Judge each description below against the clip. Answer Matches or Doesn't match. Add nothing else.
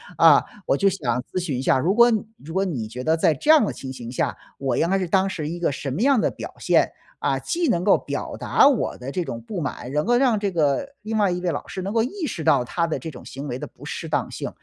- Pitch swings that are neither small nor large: Doesn't match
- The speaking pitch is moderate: Matches